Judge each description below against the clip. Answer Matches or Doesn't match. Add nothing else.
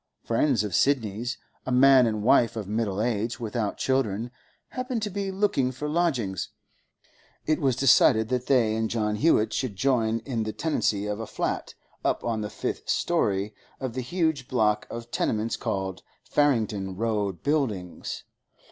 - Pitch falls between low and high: Doesn't match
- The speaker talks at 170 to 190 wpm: Doesn't match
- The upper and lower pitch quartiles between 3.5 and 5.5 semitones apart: Matches